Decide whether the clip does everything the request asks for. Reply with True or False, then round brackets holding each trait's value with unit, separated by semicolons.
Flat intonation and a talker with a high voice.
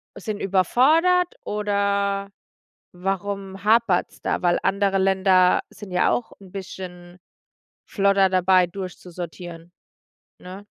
True (1.8 semitones; 195 Hz)